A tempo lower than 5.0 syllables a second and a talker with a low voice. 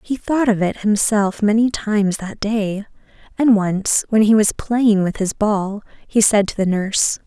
No: 4.3 syllables/s; high, 210 Hz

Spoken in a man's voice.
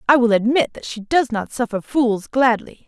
No: female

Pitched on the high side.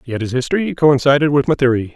No: medium, 140 Hz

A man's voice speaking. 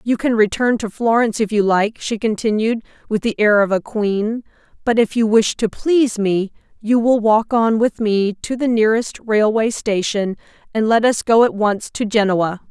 No: female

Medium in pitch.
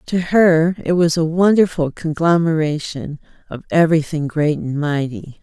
Yes: medium, 160 Hz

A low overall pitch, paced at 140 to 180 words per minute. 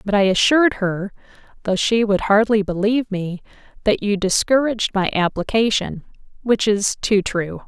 No: high, 205 Hz; average, 150 wpm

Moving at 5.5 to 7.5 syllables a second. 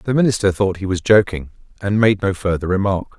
Yes: 5.6 syllables/s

